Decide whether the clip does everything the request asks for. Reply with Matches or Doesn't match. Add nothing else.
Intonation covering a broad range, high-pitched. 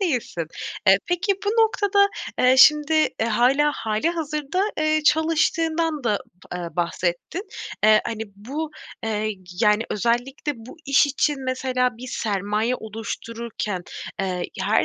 Matches